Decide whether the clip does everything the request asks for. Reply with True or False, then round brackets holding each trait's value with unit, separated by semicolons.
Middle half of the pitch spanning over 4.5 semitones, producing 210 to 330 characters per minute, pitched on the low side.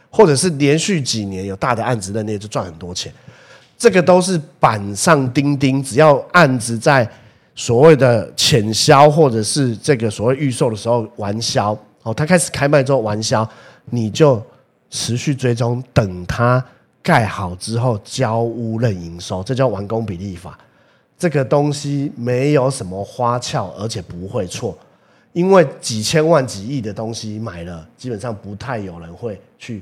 True (5.1 semitones; 245 characters per minute; 120 Hz)